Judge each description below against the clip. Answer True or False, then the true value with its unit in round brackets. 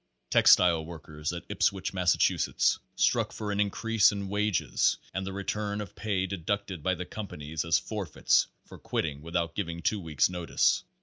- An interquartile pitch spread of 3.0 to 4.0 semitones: True (3.6 semitones)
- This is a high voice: False (95 Hz)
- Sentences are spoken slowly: False (165 wpm)